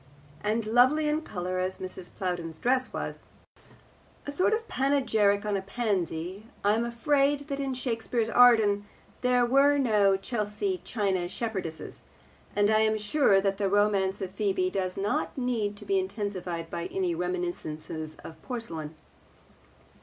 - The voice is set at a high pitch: Yes, high, 210 Hz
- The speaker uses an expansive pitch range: No, average, 4.9 semitones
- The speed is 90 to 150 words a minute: Yes, average, 145 wpm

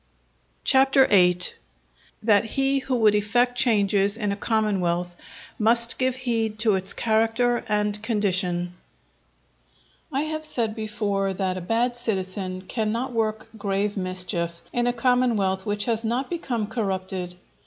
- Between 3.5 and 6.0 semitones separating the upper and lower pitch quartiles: Yes, average, 3.8 semitones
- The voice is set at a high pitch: Yes, high, 215 Hz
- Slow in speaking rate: Yes, slow, 130 wpm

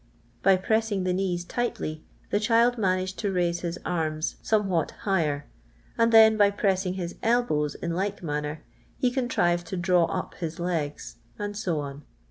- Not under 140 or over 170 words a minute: Yes, average, 165 wpm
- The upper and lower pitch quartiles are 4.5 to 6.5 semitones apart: No, average, 3.6 semitones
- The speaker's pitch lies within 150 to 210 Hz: Yes, medium, 185 Hz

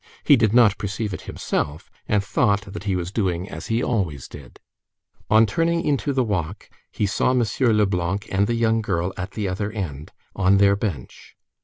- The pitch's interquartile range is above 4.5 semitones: No, average, 3.5 semitones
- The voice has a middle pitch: No, low, 100 Hz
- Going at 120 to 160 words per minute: No, average, 185 wpm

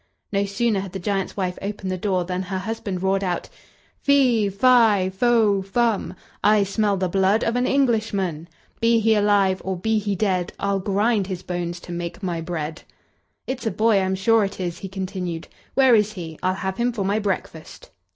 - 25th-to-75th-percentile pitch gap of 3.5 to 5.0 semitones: No, average, 2.8 semitones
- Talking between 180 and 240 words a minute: Yes, average, 190 wpm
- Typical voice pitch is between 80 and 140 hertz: No, high, 195 Hz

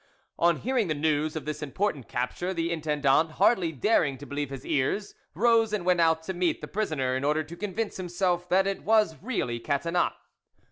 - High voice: No, medium, 165 Hz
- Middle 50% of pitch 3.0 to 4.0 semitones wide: No, average, 4.6 semitones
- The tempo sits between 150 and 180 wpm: No, average, 190 wpm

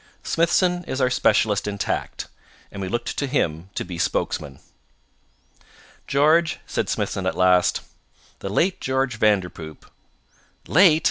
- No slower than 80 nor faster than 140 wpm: Yes, slow, 135 wpm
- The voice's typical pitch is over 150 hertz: No, low, 110 Hz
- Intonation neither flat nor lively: No, wide, 8.6 semitones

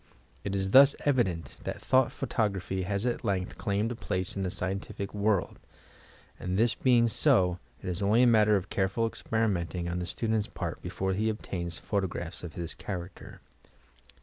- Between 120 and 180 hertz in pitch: No, low, 100 Hz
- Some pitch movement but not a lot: Yes, average, 3.5 semitones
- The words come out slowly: No, average, 175 wpm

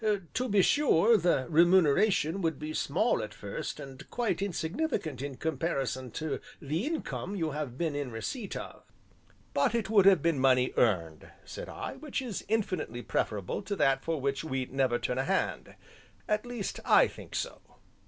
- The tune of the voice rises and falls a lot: Yes, wide, 7.2 semitones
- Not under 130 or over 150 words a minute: No, average, 175 wpm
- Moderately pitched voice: Yes, medium, 160 Hz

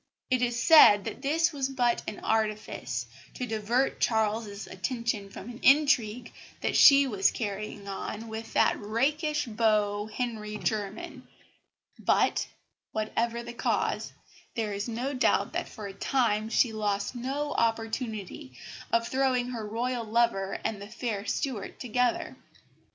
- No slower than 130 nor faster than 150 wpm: Yes, average, 140 wpm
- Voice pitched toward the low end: No, high, 225 Hz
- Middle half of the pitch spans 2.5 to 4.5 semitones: Yes, average, 2.9 semitones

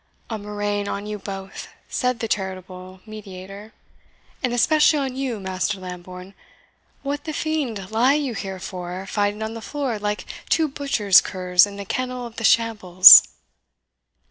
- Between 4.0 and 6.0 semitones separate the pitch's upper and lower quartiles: Yes, average, 4.5 semitones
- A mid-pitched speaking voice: No, high, 210 Hz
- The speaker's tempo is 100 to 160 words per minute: Yes, average, 150 wpm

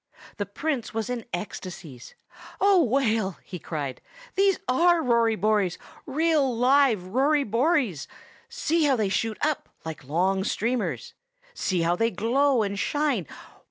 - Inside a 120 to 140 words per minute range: Yes, slow, 135 wpm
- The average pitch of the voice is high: Yes, high, 230 Hz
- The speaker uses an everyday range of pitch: No, wide, 6.9 semitones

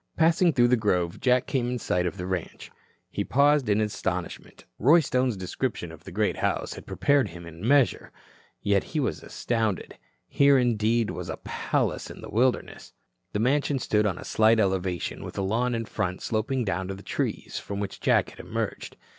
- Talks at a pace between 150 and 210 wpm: Yes, average, 195 wpm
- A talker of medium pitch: No, low, 110 Hz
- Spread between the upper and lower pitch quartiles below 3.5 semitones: No, average, 5.0 semitones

